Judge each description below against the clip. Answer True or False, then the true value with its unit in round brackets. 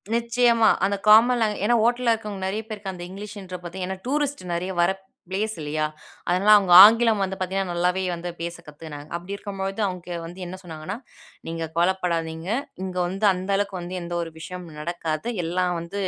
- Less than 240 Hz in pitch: True (190 Hz)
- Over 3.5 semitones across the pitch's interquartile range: False (3.2 semitones)